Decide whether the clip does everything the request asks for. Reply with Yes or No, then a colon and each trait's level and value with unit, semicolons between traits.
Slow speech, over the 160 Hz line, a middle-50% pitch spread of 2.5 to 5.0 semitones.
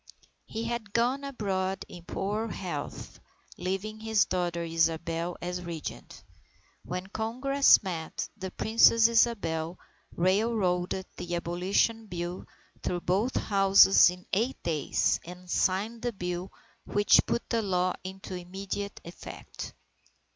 Yes: slow, 120 wpm; high, 190 Hz; average, 3.8 semitones